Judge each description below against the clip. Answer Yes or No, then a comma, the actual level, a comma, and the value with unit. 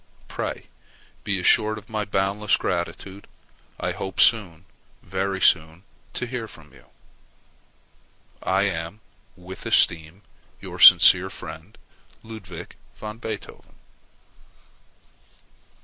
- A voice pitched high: No, very low, 95 Hz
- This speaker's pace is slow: Yes, slow, 100 wpm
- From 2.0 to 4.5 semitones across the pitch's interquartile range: Yes, average, 3.7 semitones